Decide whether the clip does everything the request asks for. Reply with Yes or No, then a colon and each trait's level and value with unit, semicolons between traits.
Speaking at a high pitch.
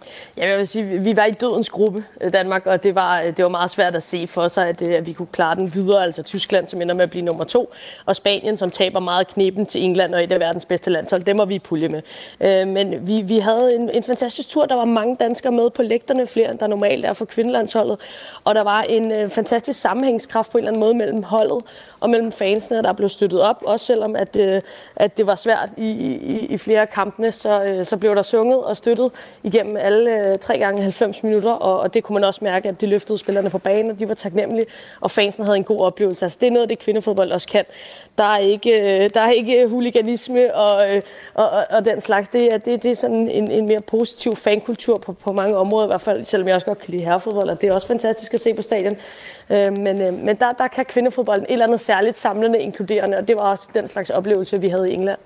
Yes: high, 210 Hz